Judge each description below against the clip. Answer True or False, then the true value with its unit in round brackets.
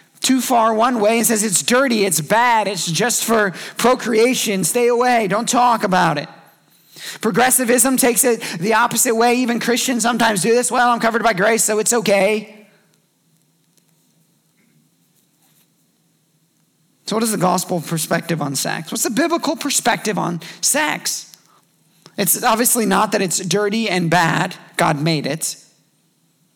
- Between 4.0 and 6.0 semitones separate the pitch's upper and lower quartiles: True (4.4 semitones)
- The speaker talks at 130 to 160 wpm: True (145 wpm)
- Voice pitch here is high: True (220 Hz)